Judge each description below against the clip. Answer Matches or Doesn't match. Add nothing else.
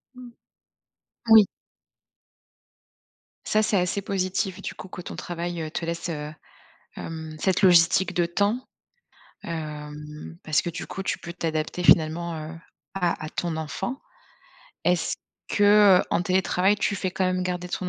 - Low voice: Doesn't match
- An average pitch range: Matches